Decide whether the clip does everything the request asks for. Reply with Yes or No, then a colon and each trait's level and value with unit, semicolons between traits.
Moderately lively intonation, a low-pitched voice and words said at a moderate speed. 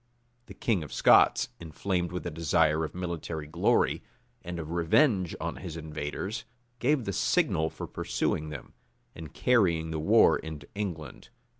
Yes: average, 3.0 semitones; very low, 85 Hz; average, 155 wpm